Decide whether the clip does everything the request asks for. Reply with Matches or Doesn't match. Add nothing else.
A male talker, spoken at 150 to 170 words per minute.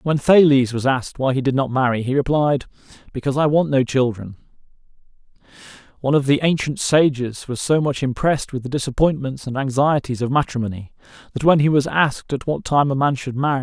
Doesn't match